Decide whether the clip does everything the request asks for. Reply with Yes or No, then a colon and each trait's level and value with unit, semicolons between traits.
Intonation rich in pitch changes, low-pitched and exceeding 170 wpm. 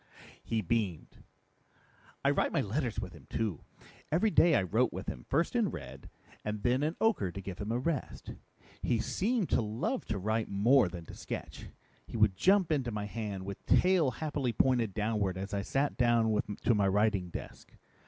Yes: wide, 5.8 semitones; low, 110 Hz; average, 185 wpm